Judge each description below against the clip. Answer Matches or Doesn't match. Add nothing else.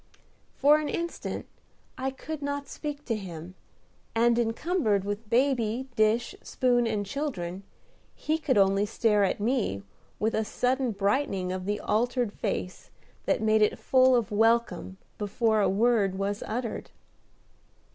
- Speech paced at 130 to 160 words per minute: Matches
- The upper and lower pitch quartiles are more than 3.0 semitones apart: Matches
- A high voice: Matches